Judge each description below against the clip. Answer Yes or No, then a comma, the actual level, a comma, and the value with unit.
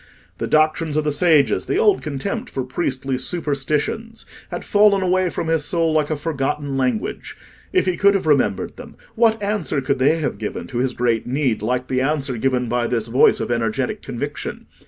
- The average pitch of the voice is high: No, medium, 145 Hz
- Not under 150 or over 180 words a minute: No, average, 190 wpm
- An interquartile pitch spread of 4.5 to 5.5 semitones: Yes, average, 4.8 semitones